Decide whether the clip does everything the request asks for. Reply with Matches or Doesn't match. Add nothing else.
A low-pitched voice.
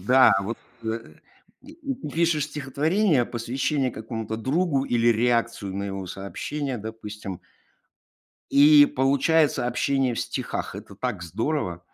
Matches